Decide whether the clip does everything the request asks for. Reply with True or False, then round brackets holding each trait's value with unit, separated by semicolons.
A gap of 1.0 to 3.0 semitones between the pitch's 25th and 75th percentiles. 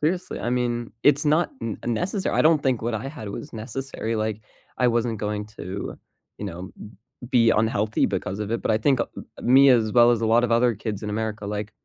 True (2.7 semitones)